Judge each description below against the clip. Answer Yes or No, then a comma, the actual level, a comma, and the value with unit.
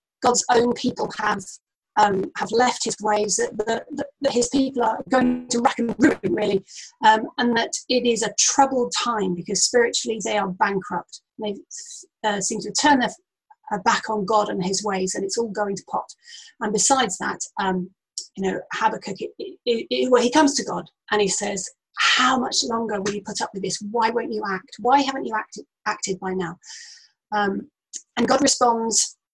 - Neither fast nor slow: Yes, average, 190 wpm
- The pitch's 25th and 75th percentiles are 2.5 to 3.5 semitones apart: No, average, 4.4 semitones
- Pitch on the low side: No, high, 225 Hz